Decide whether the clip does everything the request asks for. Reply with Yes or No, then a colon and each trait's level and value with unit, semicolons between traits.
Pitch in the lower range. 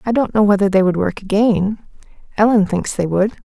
No: high, 205 Hz